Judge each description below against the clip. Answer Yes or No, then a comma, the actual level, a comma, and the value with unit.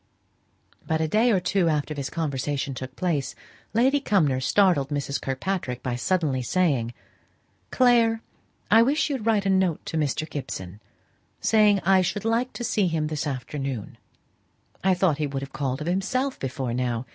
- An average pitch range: No, wide, 7.0 semitones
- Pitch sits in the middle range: Yes, medium, 160 Hz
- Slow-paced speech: No, average, 165 wpm